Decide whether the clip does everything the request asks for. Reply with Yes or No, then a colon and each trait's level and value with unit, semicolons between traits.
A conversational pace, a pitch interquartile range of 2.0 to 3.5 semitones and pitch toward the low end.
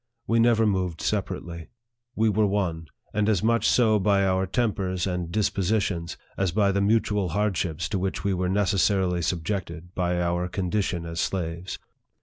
Yes: average, 160 wpm; average, 2.9 semitones; very low, 95 Hz